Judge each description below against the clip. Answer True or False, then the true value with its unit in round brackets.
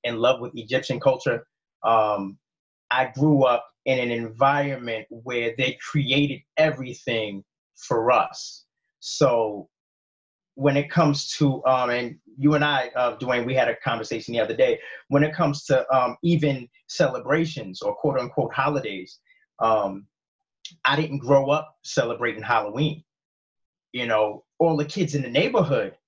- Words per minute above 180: False (145 wpm)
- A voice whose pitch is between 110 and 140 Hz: True (135 Hz)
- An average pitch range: True (3.7 semitones)